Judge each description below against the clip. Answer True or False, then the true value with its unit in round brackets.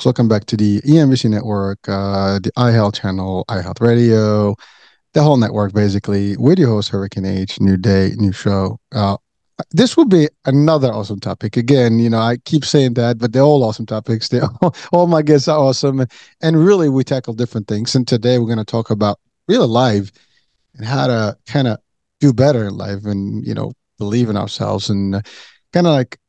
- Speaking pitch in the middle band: False (115 Hz)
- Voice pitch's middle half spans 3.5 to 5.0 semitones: True (4.6 semitones)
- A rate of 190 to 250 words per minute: True (195 wpm)